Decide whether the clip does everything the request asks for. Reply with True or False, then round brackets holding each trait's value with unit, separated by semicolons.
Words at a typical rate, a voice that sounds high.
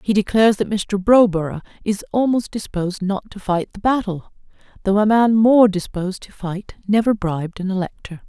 True (175 wpm; 200 Hz)